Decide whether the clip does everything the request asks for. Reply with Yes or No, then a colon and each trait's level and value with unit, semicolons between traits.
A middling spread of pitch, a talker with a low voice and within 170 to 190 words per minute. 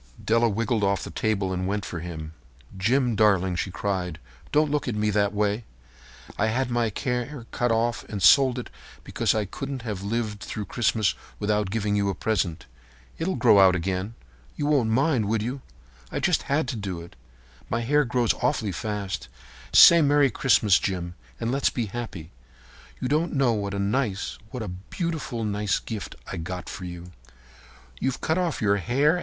Yes: average, 4.2 semitones; low, 110 Hz; average, 175 wpm